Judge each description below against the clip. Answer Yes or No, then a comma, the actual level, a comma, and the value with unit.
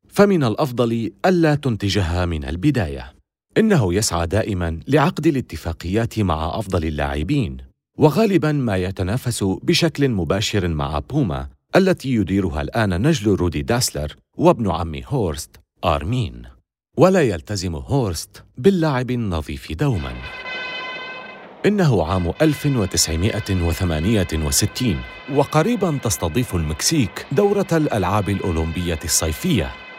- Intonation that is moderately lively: No, wide, 8.9 semitones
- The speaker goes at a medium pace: Yes, average, 95 wpm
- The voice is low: Yes, low, 100 Hz